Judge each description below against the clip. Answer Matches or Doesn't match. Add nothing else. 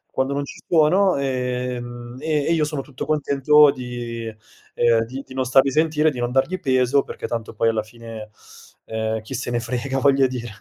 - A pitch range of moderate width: Matches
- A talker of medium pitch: Doesn't match